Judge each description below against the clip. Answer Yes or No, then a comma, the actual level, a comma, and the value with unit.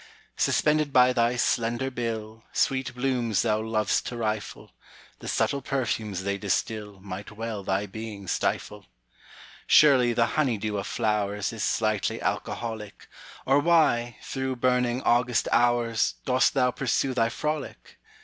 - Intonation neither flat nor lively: Yes, average, 3.0 semitones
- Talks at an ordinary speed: No, slow, 110 wpm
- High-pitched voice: No, low, 115 Hz